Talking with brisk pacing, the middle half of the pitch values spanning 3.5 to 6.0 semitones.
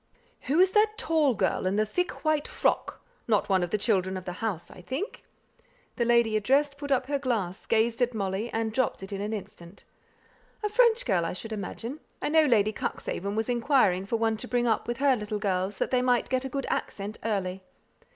Yes: fast, 215 wpm; average, 4.9 semitones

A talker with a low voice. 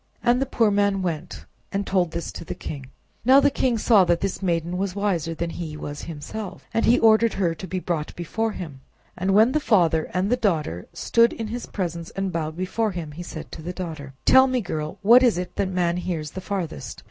No: medium, 185 Hz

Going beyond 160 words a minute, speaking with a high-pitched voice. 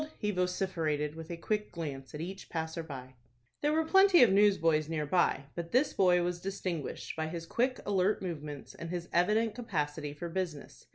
No: average, 180 wpm; medium, 175 Hz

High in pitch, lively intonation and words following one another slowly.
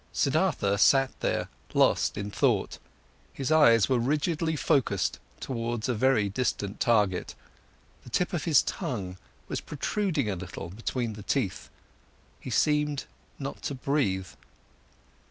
No: low, 125 Hz; wide, 6.1 semitones; slow, 130 wpm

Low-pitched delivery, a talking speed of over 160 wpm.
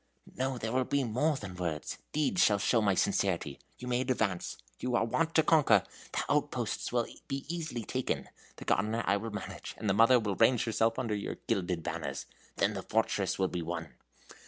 Yes: low, 115 Hz; average, 195 wpm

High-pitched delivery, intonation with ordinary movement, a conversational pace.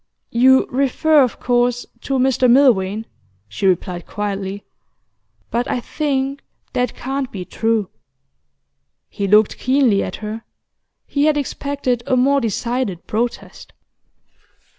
No: high, 245 Hz; average, 4.2 semitones; slow, 120 wpm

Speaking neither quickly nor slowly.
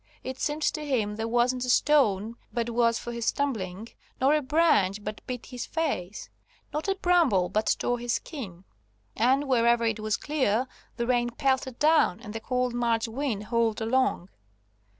Yes: average, 170 wpm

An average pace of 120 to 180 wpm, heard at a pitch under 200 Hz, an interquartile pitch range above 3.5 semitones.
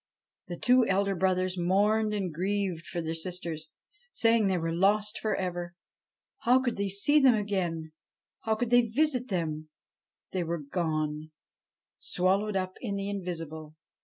Yes: average, 150 wpm; high, 190 Hz; average, 3.9 semitones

